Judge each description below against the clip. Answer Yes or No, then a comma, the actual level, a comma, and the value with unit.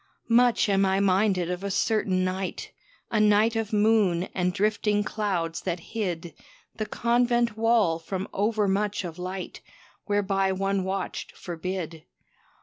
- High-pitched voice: Yes, high, 195 Hz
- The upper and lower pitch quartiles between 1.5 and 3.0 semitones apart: Yes, narrow, 2.6 semitones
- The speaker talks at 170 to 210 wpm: No, slow, 135 wpm